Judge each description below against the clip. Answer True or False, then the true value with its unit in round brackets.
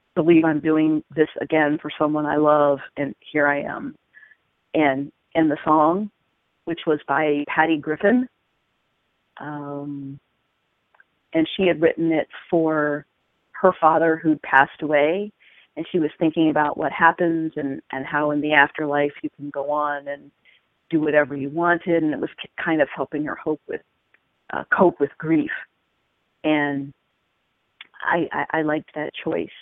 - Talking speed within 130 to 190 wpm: True (155 wpm)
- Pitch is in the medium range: True (155 Hz)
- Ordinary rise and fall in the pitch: False (2.0 semitones)